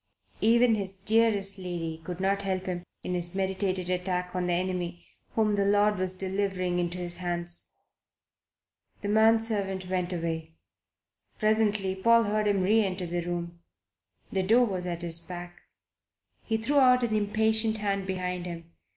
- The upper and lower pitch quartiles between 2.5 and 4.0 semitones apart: Yes, average, 3.0 semitones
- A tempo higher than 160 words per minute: No, average, 155 wpm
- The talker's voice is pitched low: No, high, 190 Hz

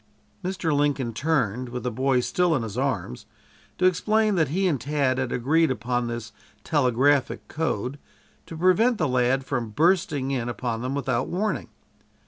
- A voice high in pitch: No, low, 135 Hz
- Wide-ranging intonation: No, average, 4.8 semitones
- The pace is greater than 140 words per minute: Yes, average, 160 wpm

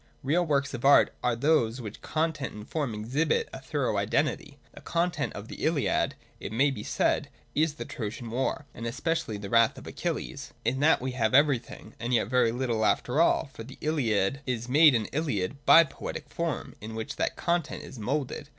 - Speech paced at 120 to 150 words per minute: No, average, 195 wpm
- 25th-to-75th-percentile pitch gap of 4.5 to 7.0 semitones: Yes, average, 4.9 semitones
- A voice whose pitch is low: Yes, low, 130 Hz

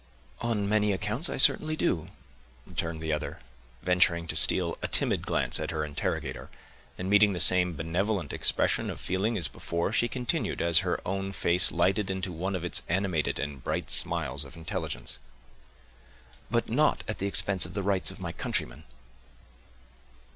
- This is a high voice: No, very low, 90 Hz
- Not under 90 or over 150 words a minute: No, average, 165 wpm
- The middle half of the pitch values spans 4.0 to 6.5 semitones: No, average, 3.4 semitones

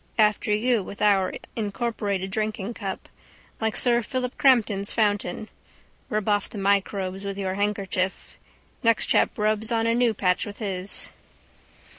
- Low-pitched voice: No, high, 210 Hz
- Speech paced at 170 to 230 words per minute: No, slow, 135 wpm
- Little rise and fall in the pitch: Yes, narrow, 2.3 semitones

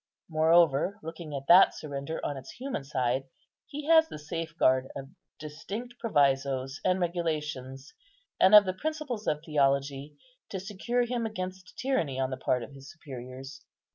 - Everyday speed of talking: Yes, average, 150 wpm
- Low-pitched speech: No, medium, 155 Hz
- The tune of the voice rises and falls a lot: Yes, wide, 5.8 semitones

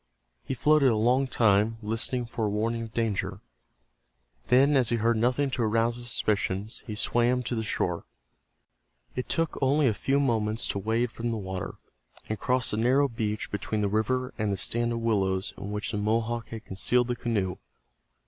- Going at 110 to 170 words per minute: No, average, 185 wpm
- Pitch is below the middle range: Yes, low, 115 Hz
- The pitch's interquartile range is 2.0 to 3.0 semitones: Yes, narrow, 2.6 semitones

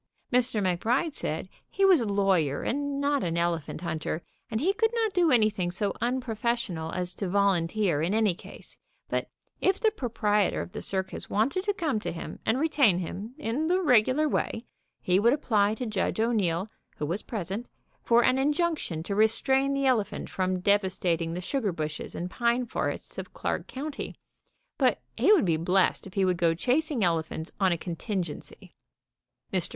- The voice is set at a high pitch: Yes, high, 215 Hz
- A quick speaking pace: No, average, 180 wpm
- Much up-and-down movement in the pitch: Yes, wide, 6.7 semitones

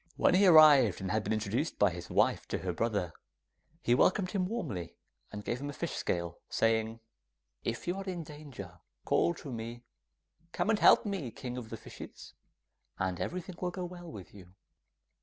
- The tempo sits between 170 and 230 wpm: Yes, average, 185 wpm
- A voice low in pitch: Yes, low, 120 Hz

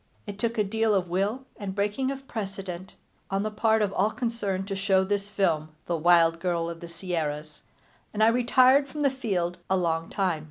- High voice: Yes, high, 195 Hz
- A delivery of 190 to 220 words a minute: Yes, average, 200 wpm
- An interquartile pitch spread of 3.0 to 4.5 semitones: Yes, average, 4.0 semitones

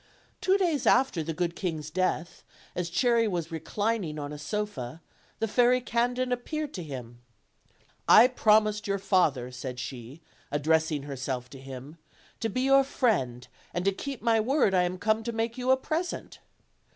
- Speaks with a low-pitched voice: No, high, 190 Hz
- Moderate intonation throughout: No, wide, 8.1 semitones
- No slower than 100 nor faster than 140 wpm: No, average, 165 wpm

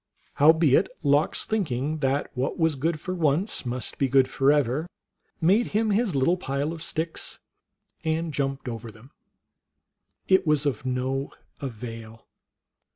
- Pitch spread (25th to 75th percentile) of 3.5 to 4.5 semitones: Yes, average, 3.9 semitones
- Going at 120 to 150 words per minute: Yes, average, 140 wpm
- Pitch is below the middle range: No, medium, 145 Hz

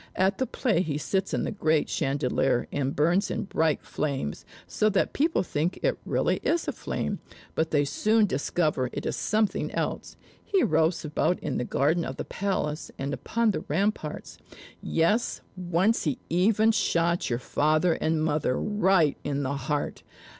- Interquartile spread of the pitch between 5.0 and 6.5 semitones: Yes, average, 5.3 semitones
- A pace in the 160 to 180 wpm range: Yes, average, 170 wpm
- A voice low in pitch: No, medium, 165 Hz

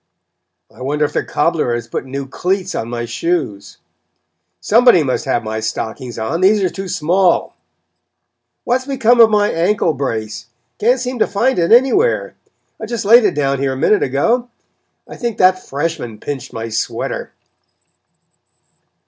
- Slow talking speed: No, average, 160 wpm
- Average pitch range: No, wide, 8.8 semitones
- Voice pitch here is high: No, medium, 170 Hz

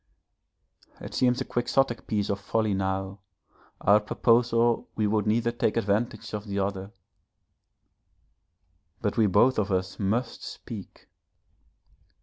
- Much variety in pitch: No, average, 2.8 semitones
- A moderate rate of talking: No, slow, 130 wpm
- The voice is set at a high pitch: No, low, 105 Hz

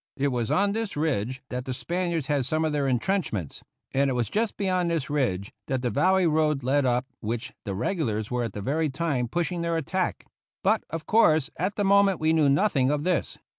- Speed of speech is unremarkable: No, fast, 210 wpm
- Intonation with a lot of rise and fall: Yes, wide, 5.8 semitones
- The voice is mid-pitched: Yes, medium, 150 Hz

